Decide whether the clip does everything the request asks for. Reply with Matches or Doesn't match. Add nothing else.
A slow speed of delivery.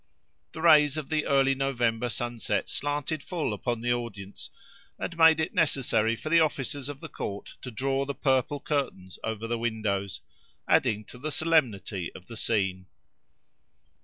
Doesn't match